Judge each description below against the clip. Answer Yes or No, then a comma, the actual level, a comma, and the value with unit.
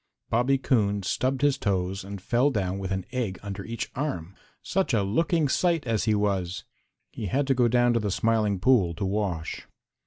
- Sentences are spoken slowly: No, average, 190 wpm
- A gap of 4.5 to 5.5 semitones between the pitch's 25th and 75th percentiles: Yes, average, 4.9 semitones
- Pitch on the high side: No, low, 110 Hz